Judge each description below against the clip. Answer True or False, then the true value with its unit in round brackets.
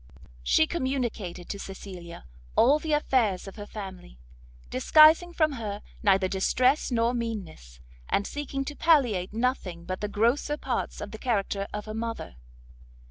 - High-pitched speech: True (220 Hz)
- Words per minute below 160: True (145 wpm)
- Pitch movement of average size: False (5.9 semitones)